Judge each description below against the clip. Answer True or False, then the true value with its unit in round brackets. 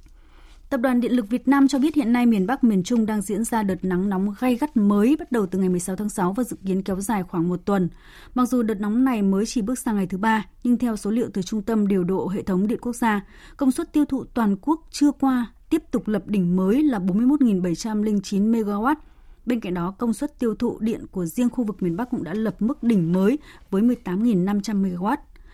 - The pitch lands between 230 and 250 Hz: False (220 Hz)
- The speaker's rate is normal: True (240 wpm)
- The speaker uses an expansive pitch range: False (4.3 semitones)